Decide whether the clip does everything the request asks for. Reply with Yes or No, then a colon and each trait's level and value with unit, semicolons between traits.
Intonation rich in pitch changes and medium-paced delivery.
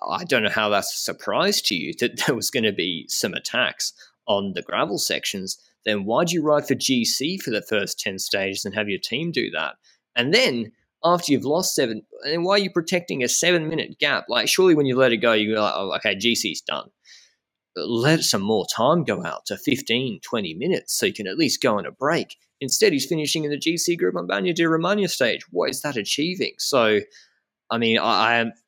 No: wide, 7.3 semitones; fast, 230 wpm